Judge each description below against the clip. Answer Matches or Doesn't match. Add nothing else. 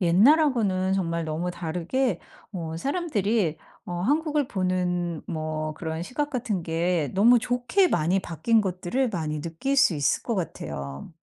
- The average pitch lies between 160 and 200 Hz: Matches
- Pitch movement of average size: Doesn't match